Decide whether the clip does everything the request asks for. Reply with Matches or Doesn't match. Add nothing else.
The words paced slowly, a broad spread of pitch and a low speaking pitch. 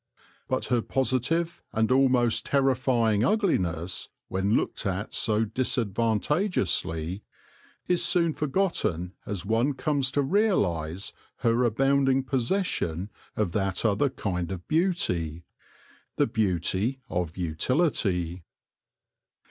Matches